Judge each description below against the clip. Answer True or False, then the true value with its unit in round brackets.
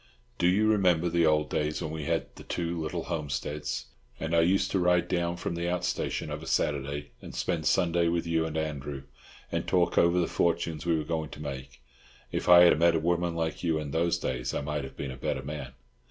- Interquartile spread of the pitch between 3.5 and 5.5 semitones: False (2.5 semitones)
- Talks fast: True (225 wpm)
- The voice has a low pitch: True (80 Hz)